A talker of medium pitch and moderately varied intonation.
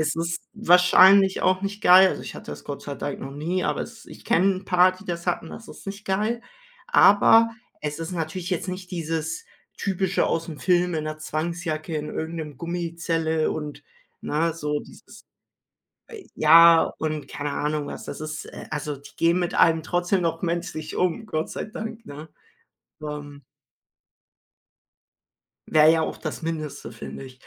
Yes: medium, 165 Hz; average, 3.0 semitones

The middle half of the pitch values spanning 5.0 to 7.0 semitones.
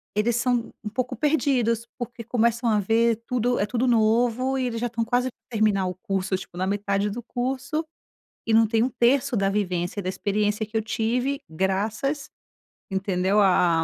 No: average, 3.4 semitones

